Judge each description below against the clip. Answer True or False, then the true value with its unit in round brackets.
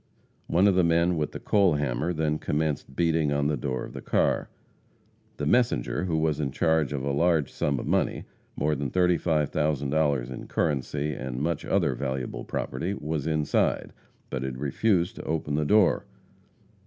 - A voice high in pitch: False (75 Hz)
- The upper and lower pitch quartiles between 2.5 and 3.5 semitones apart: True (2.9 semitones)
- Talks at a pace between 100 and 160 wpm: False (170 wpm)